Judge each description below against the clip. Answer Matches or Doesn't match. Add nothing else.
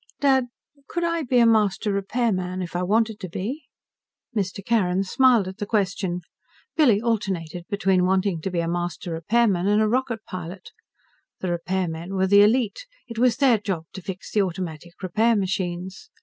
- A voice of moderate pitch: Doesn't match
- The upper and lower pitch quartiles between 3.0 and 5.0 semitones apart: Matches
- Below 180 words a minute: Matches